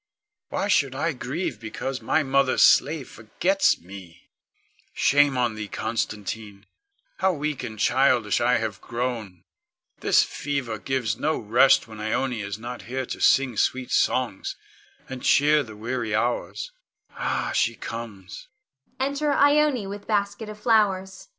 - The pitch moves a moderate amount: No, wide, 6.0 semitones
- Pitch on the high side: No, low, 130 Hz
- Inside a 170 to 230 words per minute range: No, average, 140 wpm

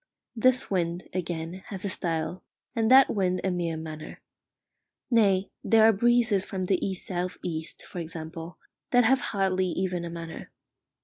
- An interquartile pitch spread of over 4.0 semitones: No, average, 3.3 semitones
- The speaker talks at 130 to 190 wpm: Yes, average, 160 wpm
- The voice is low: No, medium, 185 Hz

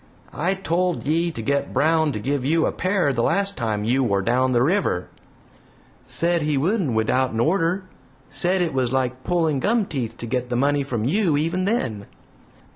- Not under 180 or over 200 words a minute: Yes, average, 185 wpm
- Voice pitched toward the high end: No, medium, 145 Hz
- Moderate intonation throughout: No, wide, 6.0 semitones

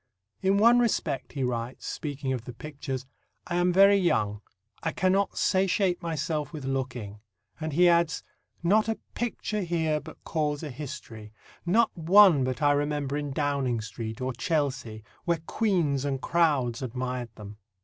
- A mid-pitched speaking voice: Yes, medium, 145 Hz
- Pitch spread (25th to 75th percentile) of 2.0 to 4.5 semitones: No, average, 5.2 semitones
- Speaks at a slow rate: No, average, 155 wpm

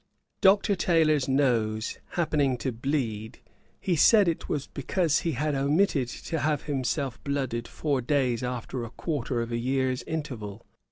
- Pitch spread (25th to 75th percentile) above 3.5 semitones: Yes, average, 4.2 semitones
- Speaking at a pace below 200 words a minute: Yes, average, 150 wpm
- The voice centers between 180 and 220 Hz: No, low, 135 Hz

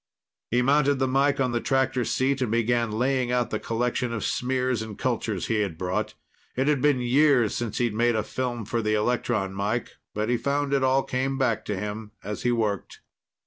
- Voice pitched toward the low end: Yes, low, 120 Hz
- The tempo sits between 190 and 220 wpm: Yes, fast, 205 wpm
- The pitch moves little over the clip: No, average, 3.3 semitones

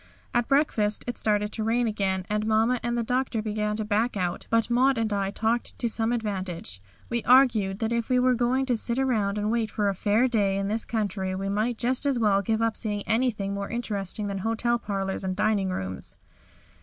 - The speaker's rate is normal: No, fast, 210 wpm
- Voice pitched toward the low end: No, high, 220 Hz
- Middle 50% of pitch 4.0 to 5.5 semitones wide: No, average, 3.0 semitones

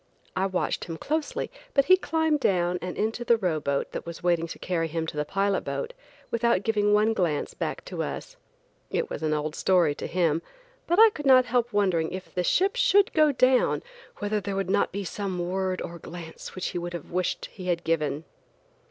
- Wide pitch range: Yes, wide, 6.0 semitones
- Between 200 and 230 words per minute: Yes, fast, 205 wpm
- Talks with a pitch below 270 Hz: Yes, high, 190 Hz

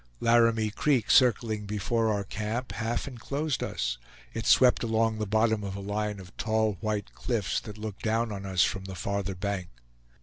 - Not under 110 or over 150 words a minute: No, average, 175 wpm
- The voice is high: No, low, 110 Hz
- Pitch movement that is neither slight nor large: No, narrow, 2.3 semitones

